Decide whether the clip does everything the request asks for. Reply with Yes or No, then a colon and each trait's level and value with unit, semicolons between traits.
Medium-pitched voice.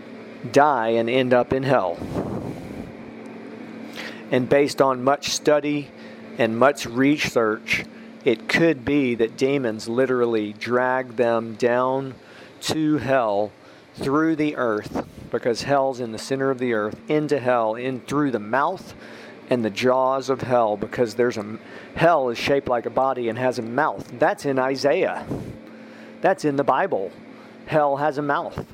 No: low, 130 Hz